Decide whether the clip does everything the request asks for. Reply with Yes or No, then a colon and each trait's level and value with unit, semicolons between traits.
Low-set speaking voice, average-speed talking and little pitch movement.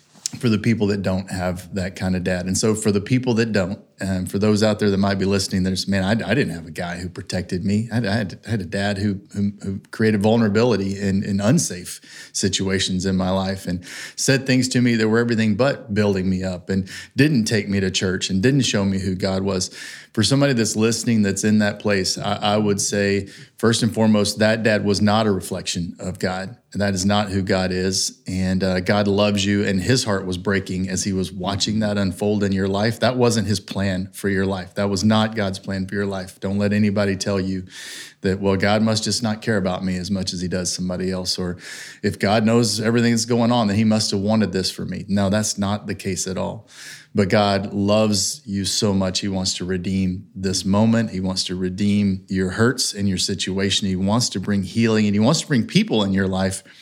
No: low, 100 Hz; fast, 235 wpm; narrow, 2.2 semitones